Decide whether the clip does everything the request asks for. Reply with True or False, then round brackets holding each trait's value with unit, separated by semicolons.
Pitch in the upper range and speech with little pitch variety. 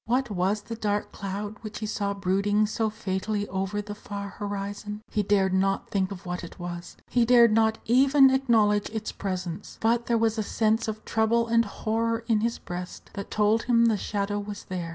True (210 Hz; 2.2 semitones)